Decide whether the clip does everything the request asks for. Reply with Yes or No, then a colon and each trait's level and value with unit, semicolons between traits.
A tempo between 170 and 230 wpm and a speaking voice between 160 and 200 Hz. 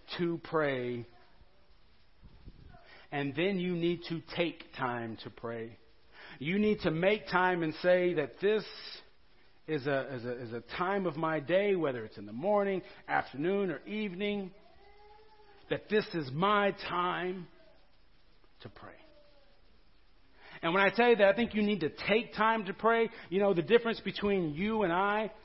No: average, 160 wpm; medium, 185 Hz